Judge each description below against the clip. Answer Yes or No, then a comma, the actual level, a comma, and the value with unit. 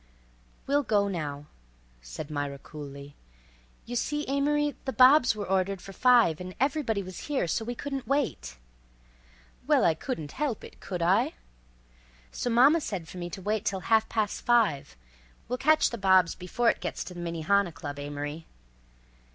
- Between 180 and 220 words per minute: No, average, 160 wpm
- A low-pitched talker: No, high, 200 Hz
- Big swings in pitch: Yes, wide, 7.3 semitones